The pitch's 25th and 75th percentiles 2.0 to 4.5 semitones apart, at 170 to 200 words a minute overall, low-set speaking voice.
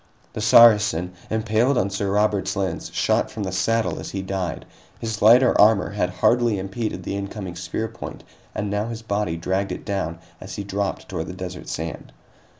Yes: average, 2.8 semitones; average, 180 wpm; low, 100 Hz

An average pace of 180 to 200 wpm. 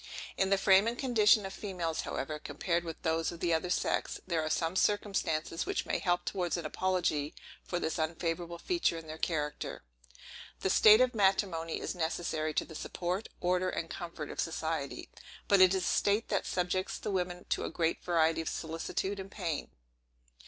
Yes: average, 185 wpm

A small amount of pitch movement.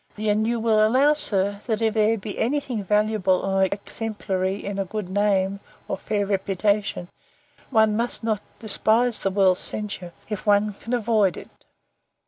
Yes: narrow, 2.1 semitones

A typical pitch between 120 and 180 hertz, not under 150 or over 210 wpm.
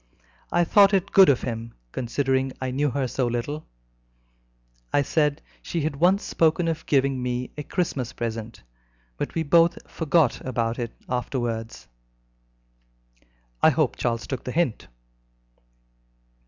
No: low, 135 Hz; average, 140 wpm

